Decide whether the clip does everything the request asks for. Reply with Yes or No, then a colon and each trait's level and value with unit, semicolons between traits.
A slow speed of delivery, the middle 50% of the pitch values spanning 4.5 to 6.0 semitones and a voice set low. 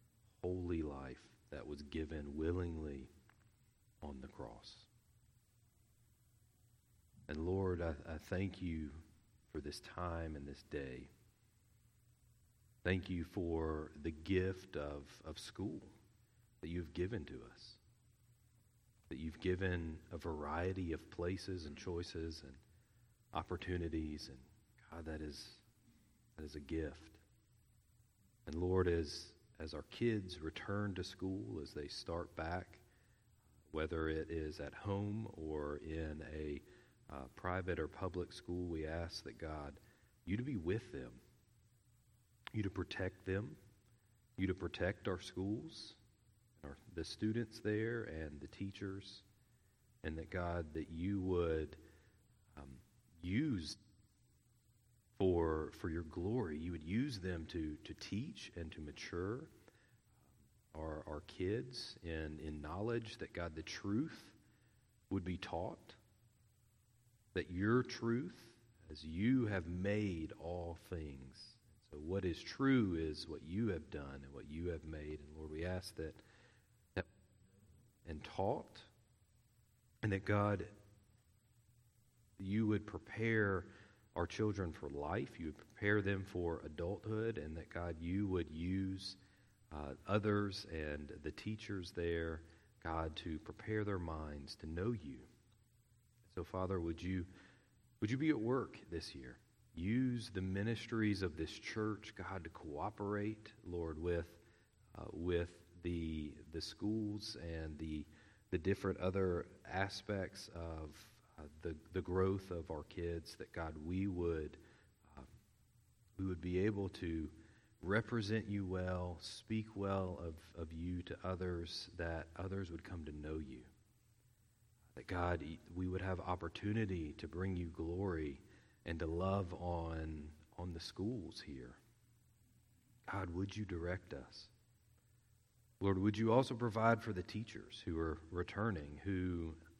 Yes: slow, 130 wpm; average, 5.1 semitones; very low, 95 Hz